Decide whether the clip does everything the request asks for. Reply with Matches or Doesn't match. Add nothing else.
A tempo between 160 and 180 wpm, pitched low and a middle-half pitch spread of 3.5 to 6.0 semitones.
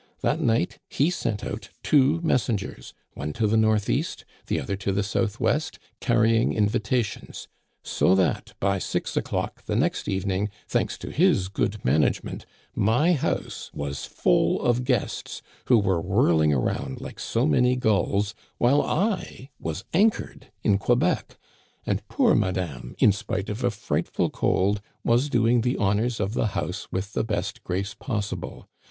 Doesn't match